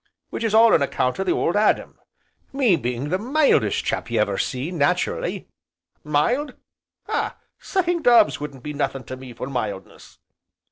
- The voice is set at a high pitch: No, medium, 155 Hz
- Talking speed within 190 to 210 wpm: No, average, 160 wpm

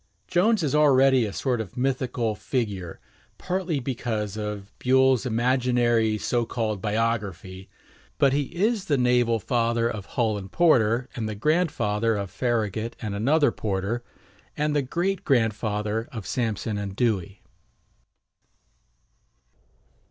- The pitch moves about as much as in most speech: Yes, average, 3.9 semitones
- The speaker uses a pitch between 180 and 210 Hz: No, low, 115 Hz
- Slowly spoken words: Yes, slow, 125 wpm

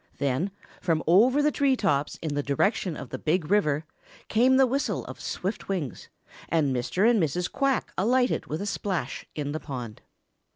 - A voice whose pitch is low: No, medium, 180 Hz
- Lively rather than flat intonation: Yes, wide, 7.9 semitones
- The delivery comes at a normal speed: Yes, average, 175 wpm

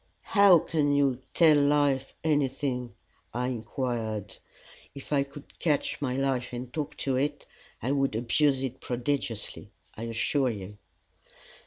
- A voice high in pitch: No, low, 135 Hz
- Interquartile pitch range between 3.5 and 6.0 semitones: No, average, 2.9 semitones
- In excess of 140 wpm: No, slow, 135 wpm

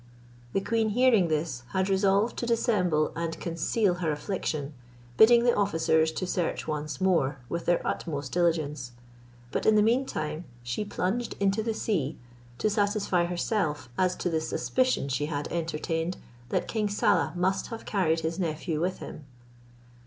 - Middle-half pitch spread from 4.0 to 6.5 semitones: Yes, average, 4.7 semitones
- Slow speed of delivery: No, average, 155 wpm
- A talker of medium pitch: Yes, medium, 175 Hz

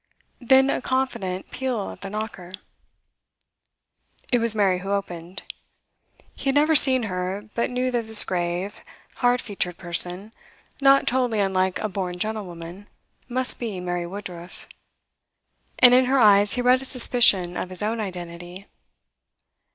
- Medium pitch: No, high, 205 Hz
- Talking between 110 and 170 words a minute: Yes, average, 145 wpm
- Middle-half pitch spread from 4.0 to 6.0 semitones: Yes, average, 5.3 semitones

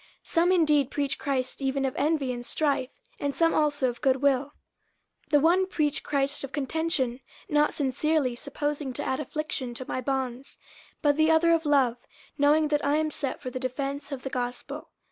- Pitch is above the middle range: Yes, very high, 280 Hz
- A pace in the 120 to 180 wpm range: No, average, 195 wpm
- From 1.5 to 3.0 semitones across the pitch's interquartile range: Yes, average, 2.7 semitones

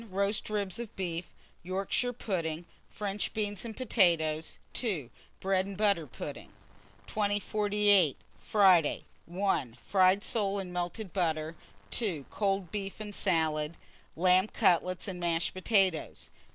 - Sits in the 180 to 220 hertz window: Yes, high, 190 Hz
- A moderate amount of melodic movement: Yes, average, 3.3 semitones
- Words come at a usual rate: No, slow, 120 wpm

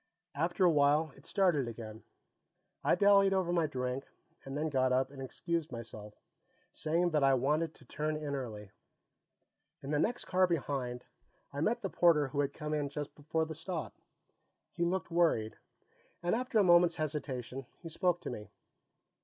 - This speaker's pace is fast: No, average, 170 wpm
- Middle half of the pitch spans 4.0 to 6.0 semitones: Yes, average, 4.3 semitones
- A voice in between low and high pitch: Yes, medium, 150 Hz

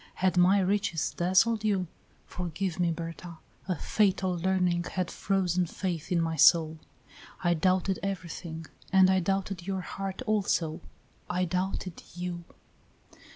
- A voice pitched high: No, medium, 180 Hz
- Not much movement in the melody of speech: Yes, narrow, 1.9 semitones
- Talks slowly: Yes, slow, 130 wpm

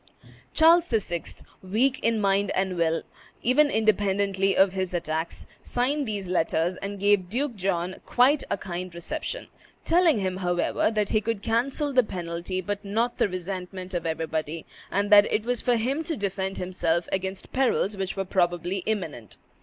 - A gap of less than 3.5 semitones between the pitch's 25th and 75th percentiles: No, average, 4.0 semitones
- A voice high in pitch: Yes, high, 195 Hz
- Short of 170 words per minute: Yes, average, 160 wpm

